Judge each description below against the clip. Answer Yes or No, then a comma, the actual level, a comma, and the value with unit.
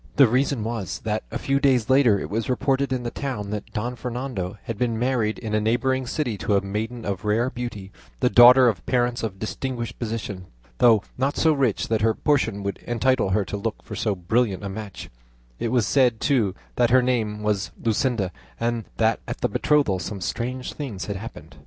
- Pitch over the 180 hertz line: No, low, 115 Hz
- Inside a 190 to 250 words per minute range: Yes, average, 200 wpm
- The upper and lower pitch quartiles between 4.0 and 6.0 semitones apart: No, average, 3.3 semitones